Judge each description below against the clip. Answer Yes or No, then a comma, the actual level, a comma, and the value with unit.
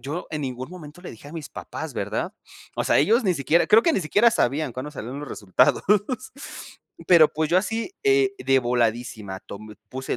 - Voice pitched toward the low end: No, medium, 150 Hz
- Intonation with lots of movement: Yes, wide, 6.4 semitones